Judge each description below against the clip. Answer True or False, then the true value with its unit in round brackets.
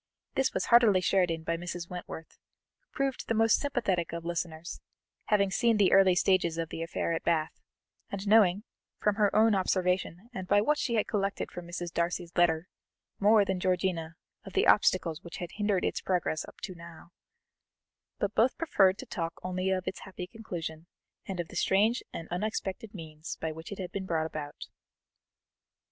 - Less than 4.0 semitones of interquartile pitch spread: True (3.4 semitones)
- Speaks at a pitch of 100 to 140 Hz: False (185 Hz)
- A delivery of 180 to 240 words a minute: True (185 wpm)